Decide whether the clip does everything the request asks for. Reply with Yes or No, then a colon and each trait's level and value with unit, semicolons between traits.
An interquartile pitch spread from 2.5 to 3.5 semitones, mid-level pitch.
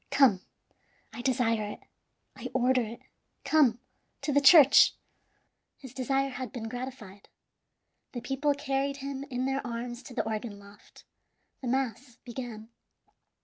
No: average, 2.9 semitones; very high, 250 Hz